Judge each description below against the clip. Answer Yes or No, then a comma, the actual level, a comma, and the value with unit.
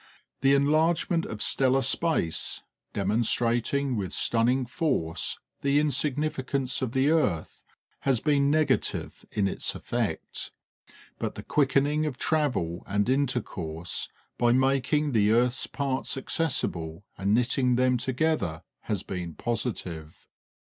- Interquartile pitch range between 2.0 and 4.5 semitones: No, average, 5.1 semitones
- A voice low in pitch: Yes, low, 130 Hz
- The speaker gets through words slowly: Yes, slow, 115 wpm